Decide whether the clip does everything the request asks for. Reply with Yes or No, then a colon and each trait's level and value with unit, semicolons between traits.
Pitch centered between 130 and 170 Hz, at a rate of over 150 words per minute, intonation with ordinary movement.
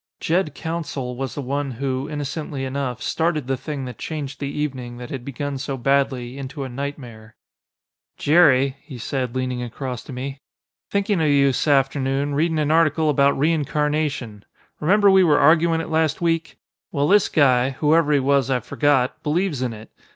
Yes: medium, 140 Hz; average, 170 wpm; average, 3.0 semitones